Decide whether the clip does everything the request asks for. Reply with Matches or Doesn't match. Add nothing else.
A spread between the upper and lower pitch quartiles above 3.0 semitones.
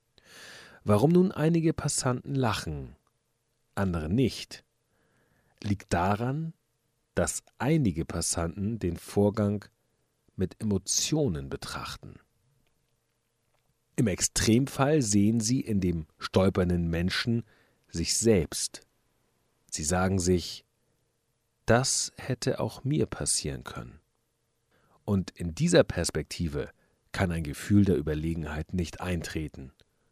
Matches